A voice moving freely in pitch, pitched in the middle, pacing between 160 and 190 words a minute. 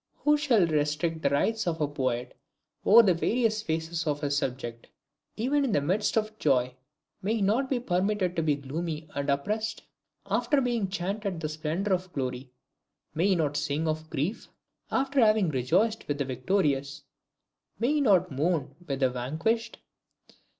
Yes: wide, 6.9 semitones; medium, 170 Hz; average, 165 wpm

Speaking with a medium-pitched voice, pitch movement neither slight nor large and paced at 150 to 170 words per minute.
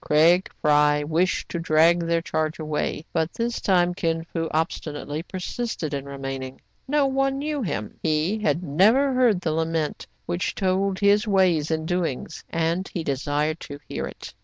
Yes: medium, 165 Hz; average, 3.7 semitones; average, 160 wpm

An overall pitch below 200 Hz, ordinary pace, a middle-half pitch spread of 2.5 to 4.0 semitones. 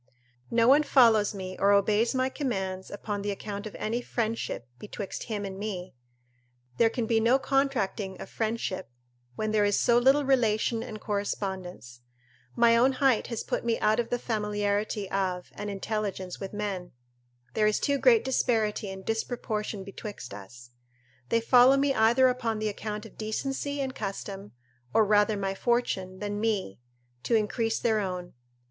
No: high, 215 Hz; average, 165 wpm; average, 3.0 semitones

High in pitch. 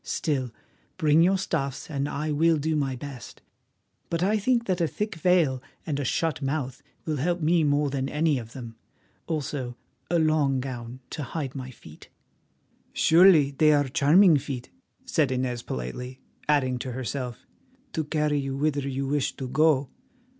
No: medium, 145 Hz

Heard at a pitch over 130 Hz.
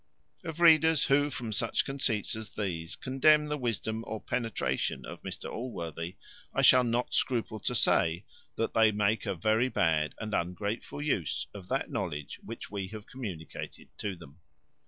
No: low, 110 Hz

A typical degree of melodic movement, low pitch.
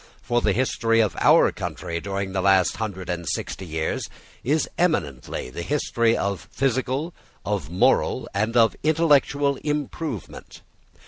No: wide, 6.9 semitones; low, 115 Hz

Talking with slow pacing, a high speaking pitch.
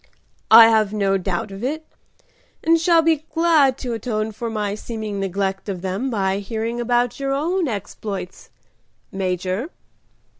No: average, 145 wpm; high, 220 Hz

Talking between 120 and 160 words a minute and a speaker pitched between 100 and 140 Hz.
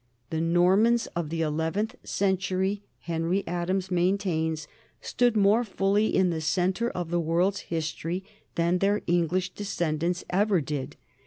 No: slow, 135 wpm; medium, 180 Hz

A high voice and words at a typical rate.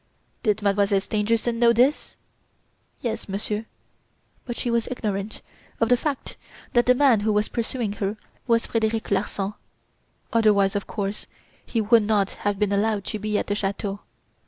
Yes: high, 215 Hz; average, 155 wpm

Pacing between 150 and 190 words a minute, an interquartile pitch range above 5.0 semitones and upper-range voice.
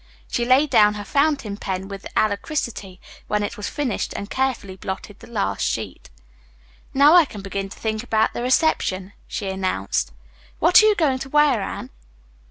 Yes: average, 175 wpm; wide, 5.6 semitones; high, 215 Hz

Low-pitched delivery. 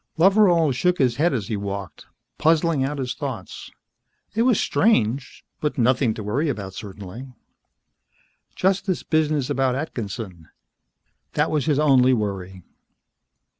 Yes: low, 130 Hz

